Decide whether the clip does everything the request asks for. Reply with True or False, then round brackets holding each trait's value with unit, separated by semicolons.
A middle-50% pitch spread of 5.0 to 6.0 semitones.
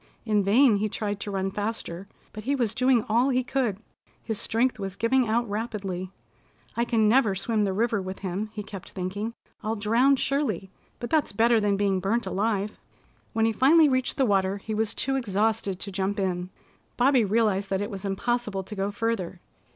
False (3.3 semitones)